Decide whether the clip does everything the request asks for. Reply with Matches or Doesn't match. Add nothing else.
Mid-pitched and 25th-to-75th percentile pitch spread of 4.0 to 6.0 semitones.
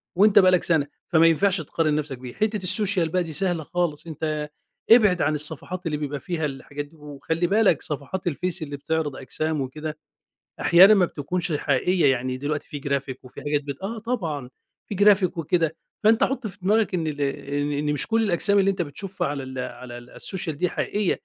Matches